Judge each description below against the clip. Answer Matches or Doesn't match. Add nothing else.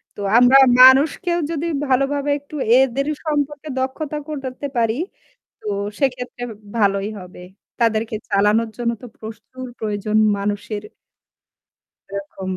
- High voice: Matches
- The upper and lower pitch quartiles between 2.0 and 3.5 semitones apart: Doesn't match